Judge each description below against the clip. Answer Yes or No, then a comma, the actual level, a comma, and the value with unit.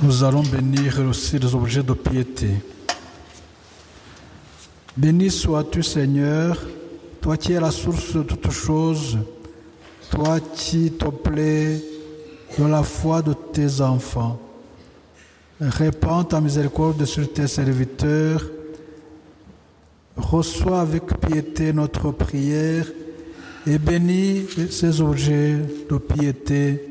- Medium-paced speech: No, slow, 105 wpm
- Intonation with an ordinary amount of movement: Yes, average, 3.5 semitones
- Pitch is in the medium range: Yes, medium, 150 Hz